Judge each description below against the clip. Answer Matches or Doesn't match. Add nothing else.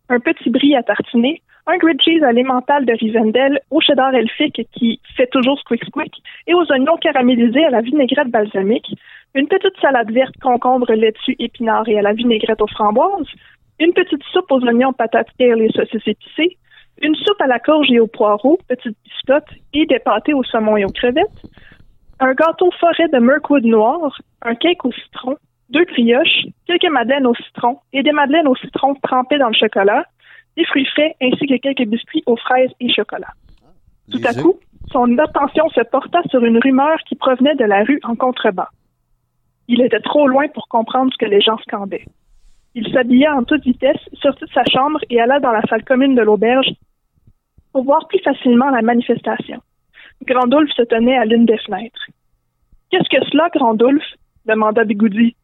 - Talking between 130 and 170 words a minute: Doesn't match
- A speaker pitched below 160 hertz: Doesn't match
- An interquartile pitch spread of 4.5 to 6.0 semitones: Doesn't match